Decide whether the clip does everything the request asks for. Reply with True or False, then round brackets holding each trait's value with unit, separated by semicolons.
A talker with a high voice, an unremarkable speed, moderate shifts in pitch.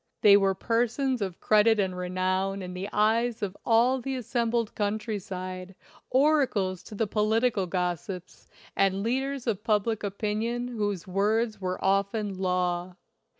True (205 Hz; 145 wpm; 3.5 semitones)